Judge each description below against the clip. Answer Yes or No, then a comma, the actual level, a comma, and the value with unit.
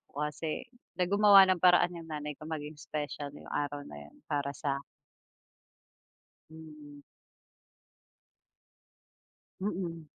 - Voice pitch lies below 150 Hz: No, medium, 155 Hz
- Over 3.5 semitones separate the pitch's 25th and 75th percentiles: No, average, 3.2 semitones